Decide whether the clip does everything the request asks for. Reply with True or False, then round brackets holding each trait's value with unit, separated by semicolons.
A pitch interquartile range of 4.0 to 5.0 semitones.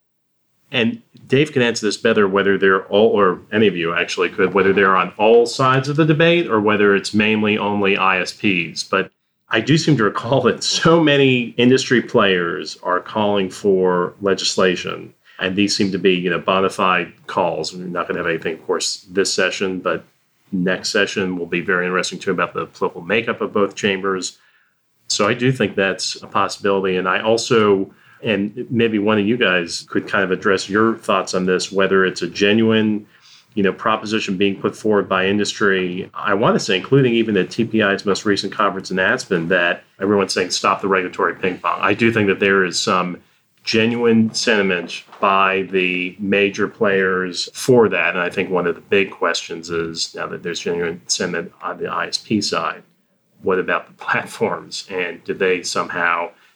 False (3.1 semitones)